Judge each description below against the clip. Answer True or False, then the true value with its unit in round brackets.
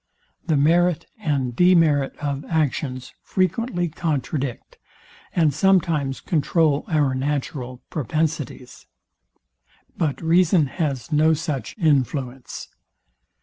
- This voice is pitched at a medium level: True (150 Hz)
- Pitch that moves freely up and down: False (3.5 semitones)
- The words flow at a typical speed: False (90 wpm)